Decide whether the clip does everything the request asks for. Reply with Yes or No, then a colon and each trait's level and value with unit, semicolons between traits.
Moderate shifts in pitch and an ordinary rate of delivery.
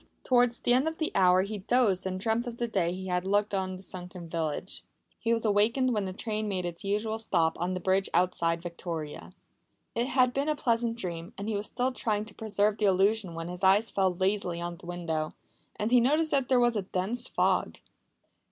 No: average, 4.4 semitones; fast, 215 wpm